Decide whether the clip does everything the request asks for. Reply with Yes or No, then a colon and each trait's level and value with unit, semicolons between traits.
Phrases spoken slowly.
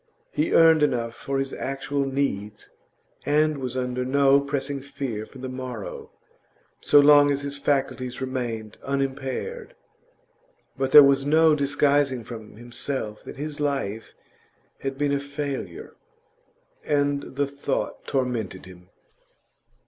Yes: slow, 125 wpm